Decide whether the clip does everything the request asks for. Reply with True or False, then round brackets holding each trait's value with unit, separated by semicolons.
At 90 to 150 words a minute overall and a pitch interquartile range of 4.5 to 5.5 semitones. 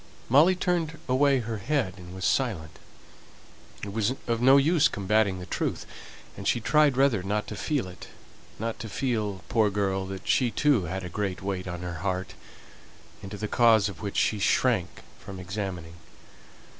False (170 wpm; 5.1 semitones)